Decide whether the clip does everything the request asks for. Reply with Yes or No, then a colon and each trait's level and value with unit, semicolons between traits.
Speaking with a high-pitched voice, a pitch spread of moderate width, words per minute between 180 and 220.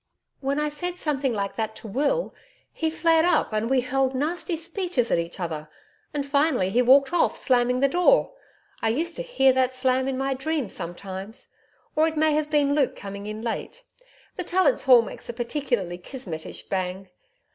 No: very high, 265 Hz; wide, 5.8 semitones; average, 190 wpm